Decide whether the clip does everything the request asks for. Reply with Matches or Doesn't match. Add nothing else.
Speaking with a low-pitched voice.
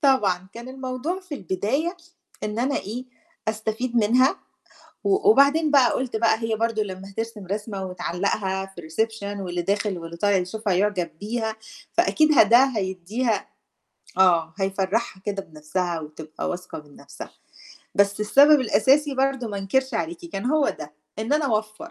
Doesn't match